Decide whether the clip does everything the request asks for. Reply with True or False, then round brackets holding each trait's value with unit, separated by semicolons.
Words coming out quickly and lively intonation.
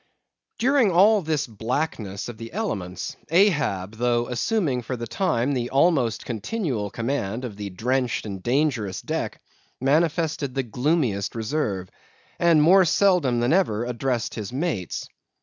False (135 wpm; 6.4 semitones)